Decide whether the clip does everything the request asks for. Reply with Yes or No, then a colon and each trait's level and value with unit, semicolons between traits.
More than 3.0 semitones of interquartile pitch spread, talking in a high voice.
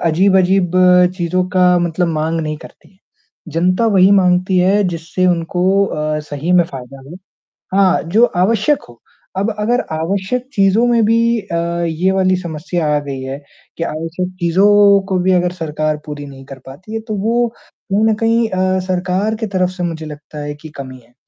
No: average, 3.7 semitones; medium, 180 Hz